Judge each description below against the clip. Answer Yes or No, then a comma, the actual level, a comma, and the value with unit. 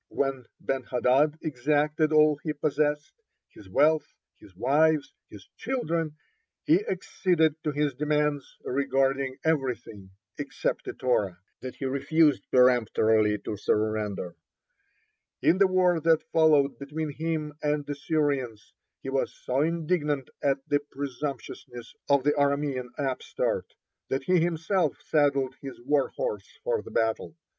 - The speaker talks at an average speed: No, slow, 130 wpm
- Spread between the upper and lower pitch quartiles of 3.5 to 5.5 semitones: No, average, 3.0 semitones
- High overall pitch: No, medium, 145 Hz